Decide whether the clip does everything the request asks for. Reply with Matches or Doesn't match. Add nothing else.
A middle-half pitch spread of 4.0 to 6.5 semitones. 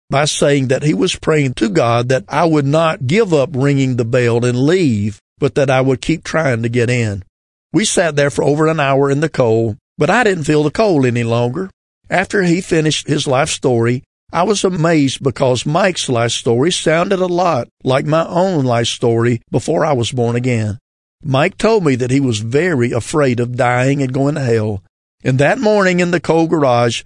Matches